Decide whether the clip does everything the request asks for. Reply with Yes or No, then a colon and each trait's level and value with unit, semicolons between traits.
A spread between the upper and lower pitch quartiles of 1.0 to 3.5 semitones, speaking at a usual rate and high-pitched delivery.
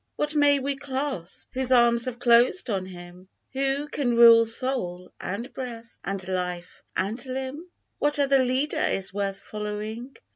No: wide, 5.4 semitones; average, 150 wpm; high, 240 Hz